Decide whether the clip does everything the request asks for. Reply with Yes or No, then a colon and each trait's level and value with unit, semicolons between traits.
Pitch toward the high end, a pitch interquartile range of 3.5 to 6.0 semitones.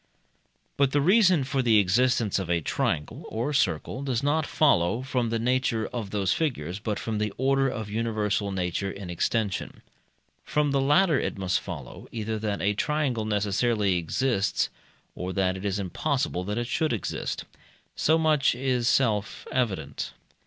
No: low, 115 Hz; average, 5.3 semitones